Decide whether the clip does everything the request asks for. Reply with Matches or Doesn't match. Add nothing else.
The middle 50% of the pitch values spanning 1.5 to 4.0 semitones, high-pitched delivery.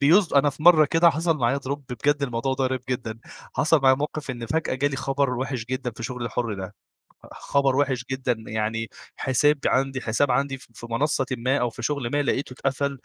Doesn't match